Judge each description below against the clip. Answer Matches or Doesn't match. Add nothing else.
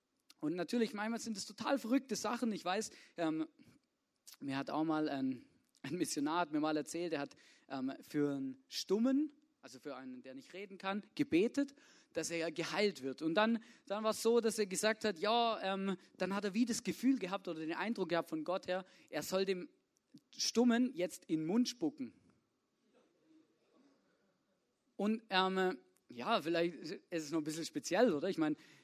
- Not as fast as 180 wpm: Doesn't match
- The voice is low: Doesn't match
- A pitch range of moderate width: Doesn't match